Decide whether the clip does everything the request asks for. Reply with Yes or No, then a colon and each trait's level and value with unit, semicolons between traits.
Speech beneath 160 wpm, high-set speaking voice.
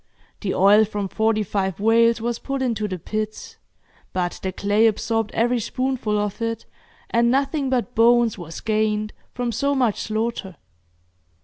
Yes: average, 150 wpm; high, 220 Hz